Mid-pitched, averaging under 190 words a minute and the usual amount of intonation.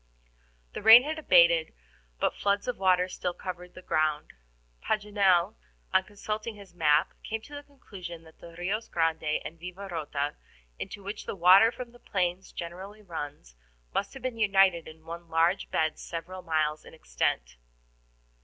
Yes: medium, 180 Hz; average, 155 wpm; average, 3.8 semitones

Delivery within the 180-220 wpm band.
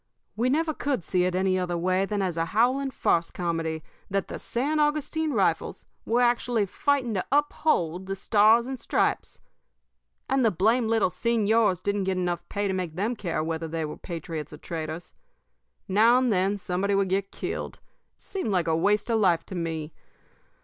Yes: average, 185 wpm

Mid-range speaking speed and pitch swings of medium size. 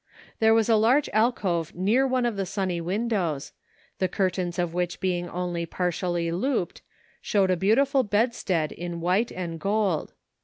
Yes: average, 155 wpm; average, 4.1 semitones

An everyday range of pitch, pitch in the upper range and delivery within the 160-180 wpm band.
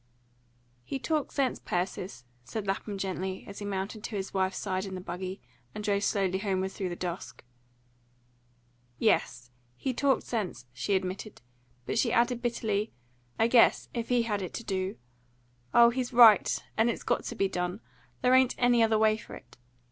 Yes: average, 3.7 semitones; high, 205 Hz; average, 175 wpm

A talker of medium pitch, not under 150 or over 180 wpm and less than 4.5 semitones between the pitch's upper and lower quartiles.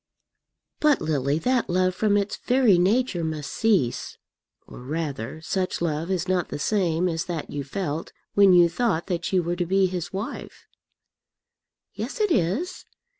Yes: medium, 180 Hz; average, 160 wpm; average, 3.9 semitones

